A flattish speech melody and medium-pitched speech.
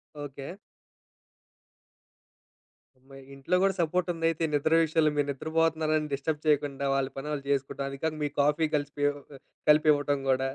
Yes: narrow, 2.3 semitones; medium, 150 Hz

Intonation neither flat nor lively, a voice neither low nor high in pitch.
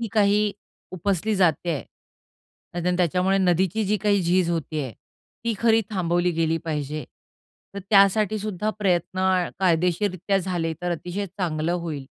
Yes: average, 3.1 semitones; medium, 180 Hz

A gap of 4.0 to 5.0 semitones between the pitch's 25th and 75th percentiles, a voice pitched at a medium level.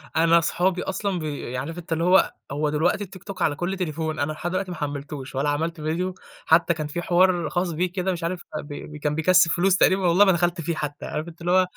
No: average, 3.1 semitones; medium, 170 Hz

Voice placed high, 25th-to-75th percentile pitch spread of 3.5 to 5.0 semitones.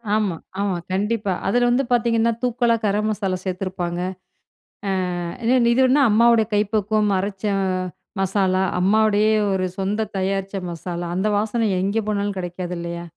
No: high, 205 Hz; average, 2.8 semitones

